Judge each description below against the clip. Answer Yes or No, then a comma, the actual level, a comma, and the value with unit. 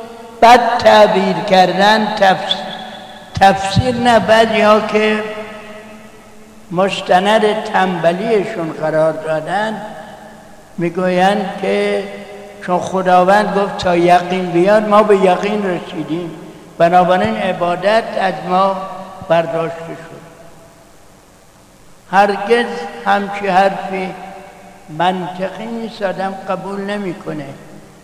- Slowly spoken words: Yes, slow, 80 wpm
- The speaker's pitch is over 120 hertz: Yes, high, 190 Hz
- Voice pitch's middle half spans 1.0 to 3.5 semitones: Yes, average, 2.7 semitones